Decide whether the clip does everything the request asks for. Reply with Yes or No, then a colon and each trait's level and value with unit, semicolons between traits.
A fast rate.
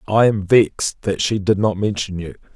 Yes: fast, 210 wpm